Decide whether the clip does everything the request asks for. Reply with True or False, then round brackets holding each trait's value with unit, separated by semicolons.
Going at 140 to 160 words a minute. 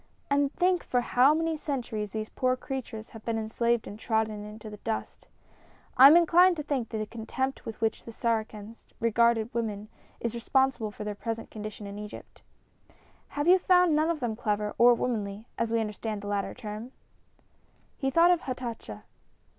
False (175 wpm)